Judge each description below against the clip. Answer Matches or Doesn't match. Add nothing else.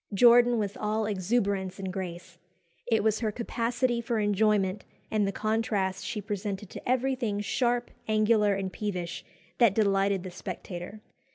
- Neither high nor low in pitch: Doesn't match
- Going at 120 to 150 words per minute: Matches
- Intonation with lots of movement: Doesn't match